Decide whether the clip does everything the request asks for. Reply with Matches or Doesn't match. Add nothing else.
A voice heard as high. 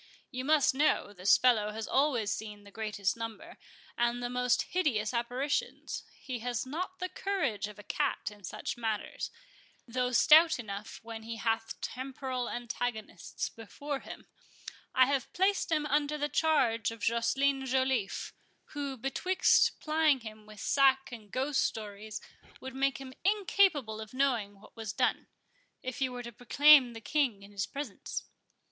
Matches